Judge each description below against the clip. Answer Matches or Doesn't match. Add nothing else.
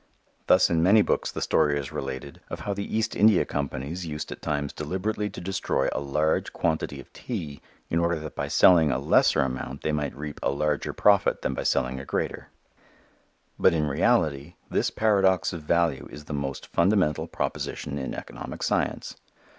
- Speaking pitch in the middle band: Doesn't match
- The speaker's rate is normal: Matches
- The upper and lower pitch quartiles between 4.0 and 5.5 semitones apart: Matches